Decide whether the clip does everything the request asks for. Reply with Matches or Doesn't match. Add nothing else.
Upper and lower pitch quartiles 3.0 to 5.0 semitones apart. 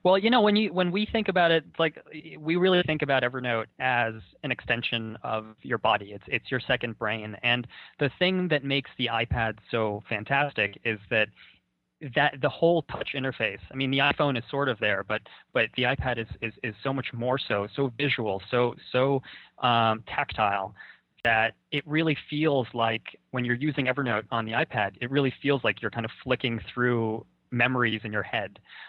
Matches